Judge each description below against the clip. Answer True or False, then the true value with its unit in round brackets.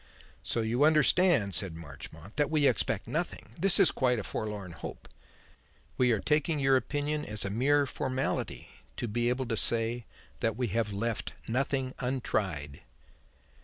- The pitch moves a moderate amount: True (4.7 semitones)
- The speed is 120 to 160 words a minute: True (155 wpm)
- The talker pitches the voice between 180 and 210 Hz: False (120 Hz)